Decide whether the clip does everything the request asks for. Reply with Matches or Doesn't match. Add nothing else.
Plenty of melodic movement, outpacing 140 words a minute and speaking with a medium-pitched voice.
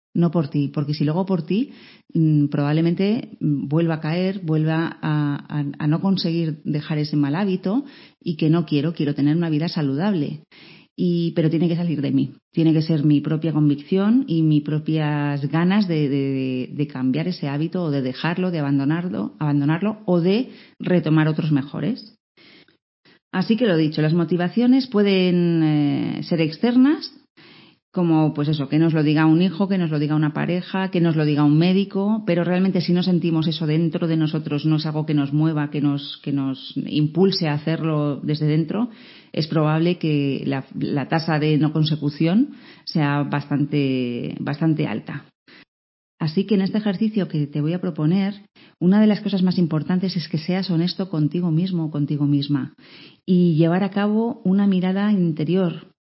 Doesn't match